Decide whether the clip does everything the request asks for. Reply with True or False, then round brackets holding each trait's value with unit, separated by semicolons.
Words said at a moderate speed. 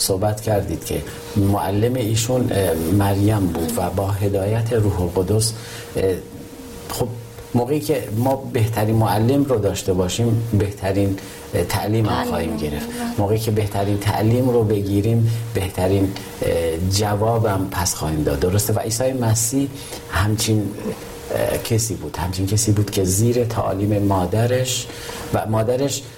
True (120 wpm)